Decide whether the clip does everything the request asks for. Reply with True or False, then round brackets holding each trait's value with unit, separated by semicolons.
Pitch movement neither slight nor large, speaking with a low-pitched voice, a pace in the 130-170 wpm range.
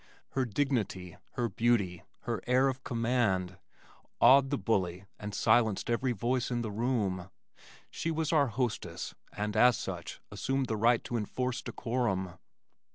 True (4.0 semitones; 120 Hz; 145 wpm)